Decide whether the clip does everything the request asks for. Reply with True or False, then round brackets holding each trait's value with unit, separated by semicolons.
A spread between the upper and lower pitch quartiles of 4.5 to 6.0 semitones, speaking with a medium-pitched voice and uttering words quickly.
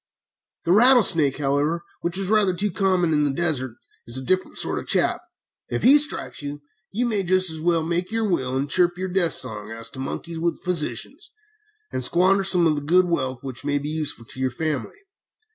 True (4.9 semitones; 170 Hz; 210 wpm)